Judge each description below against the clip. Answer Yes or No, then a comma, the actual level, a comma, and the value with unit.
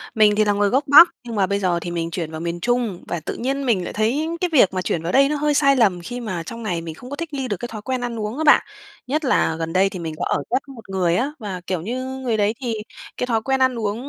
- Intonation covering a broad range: Yes, wide, 6.0 semitones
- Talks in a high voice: Yes, high, 215 Hz